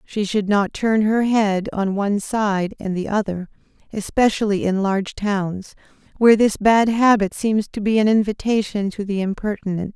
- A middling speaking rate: Yes, average, 170 wpm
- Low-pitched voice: No, high, 205 Hz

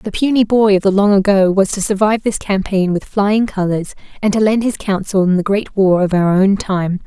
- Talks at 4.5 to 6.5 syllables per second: Yes, 5.2 syllables/s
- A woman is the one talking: Yes, female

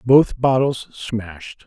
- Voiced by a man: Yes, male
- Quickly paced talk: No, slow, 110 wpm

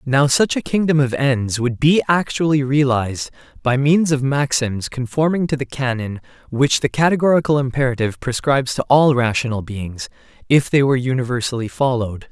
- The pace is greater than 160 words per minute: No, average, 155 wpm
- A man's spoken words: Yes, male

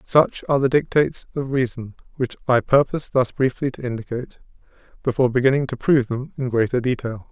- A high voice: No, low, 130 Hz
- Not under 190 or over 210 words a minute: No, average, 170 wpm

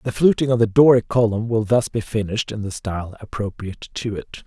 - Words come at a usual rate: No, fast, 215 wpm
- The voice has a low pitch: Yes, low, 110 Hz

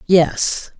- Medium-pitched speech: Yes, medium, 175 Hz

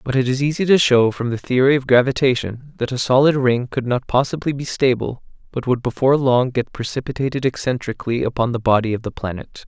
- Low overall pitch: Yes, low, 125 Hz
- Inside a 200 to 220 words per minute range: Yes, fast, 205 wpm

